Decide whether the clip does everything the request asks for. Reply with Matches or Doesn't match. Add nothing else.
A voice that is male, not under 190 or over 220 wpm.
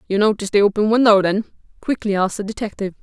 Doesn't match